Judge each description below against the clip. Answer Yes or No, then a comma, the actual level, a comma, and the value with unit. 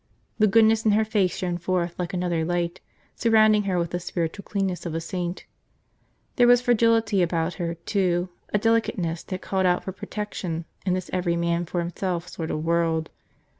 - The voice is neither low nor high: Yes, medium, 180 Hz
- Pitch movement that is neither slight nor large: Yes, average, 3.4 semitones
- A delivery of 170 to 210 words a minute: Yes, average, 180 wpm